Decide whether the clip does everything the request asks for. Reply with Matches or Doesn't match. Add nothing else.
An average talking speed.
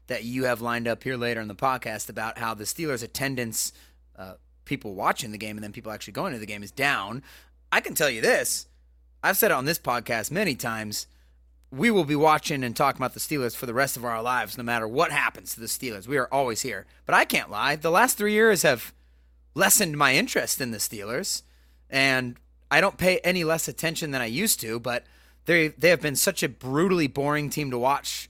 Doesn't match